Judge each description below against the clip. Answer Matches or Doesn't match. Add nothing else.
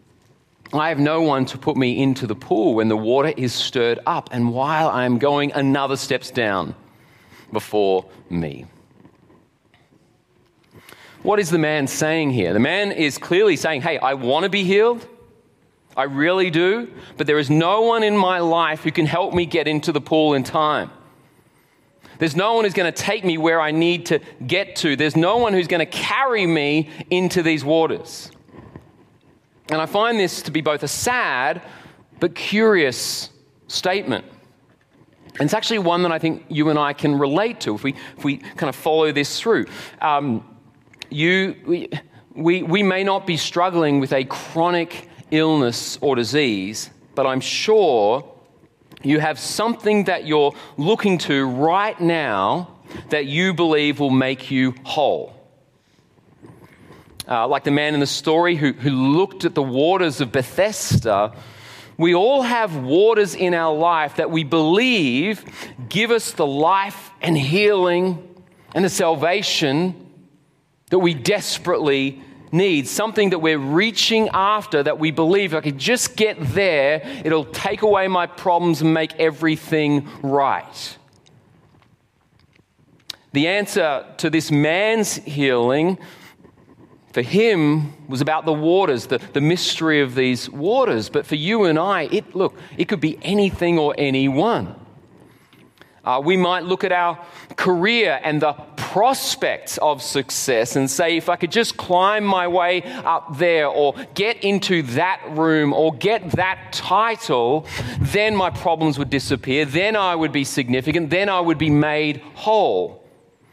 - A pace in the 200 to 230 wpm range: Doesn't match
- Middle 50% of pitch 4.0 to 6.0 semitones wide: Matches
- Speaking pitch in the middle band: Matches